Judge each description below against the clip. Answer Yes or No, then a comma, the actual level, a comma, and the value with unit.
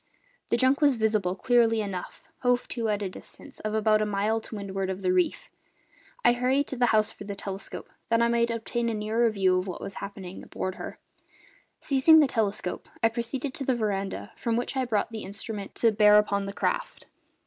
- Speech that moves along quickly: Yes, fast, 210 wpm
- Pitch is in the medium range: No, high, 220 Hz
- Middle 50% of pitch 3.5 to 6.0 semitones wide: No, average, 3.1 semitones